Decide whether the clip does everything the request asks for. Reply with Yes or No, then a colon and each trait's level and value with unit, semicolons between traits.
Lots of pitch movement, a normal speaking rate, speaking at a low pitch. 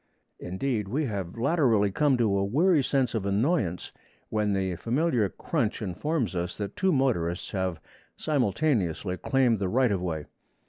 Yes: wide, 6.2 semitones; average, 150 wpm; low, 110 Hz